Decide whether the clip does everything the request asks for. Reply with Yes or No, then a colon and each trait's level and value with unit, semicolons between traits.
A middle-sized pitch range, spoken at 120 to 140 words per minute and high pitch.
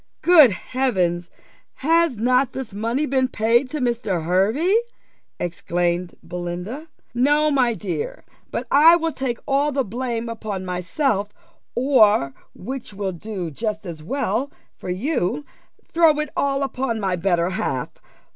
No: wide, 6.9 semitones; slow, 135 wpm; high, 230 Hz